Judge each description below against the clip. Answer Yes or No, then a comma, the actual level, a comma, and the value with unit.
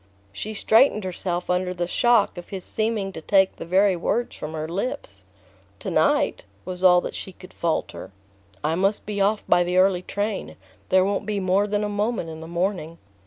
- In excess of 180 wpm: Yes, average, 195 wpm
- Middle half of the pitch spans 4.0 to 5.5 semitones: No, average, 2.7 semitones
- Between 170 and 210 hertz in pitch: Yes, high, 190 Hz